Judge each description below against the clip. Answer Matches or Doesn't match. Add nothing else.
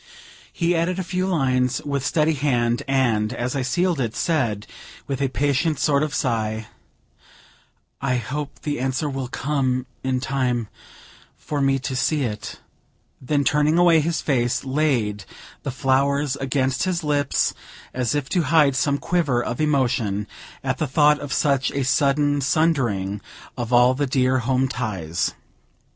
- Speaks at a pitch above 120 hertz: Matches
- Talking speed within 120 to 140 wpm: Doesn't match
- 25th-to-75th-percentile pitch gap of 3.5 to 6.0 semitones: Doesn't match